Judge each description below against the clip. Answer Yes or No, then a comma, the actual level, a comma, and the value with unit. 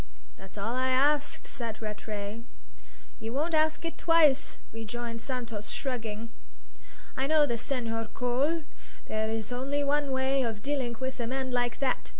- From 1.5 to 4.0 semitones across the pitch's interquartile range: Yes, average, 3.7 semitones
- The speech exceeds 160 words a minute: No, average, 155 wpm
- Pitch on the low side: No, very high, 250 Hz